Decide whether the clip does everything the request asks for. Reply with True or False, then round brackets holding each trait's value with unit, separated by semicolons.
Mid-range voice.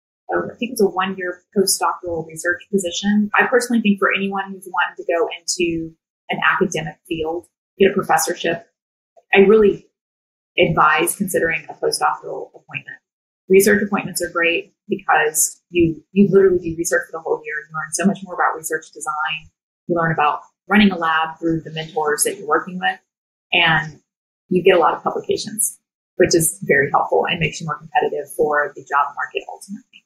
True (180 Hz)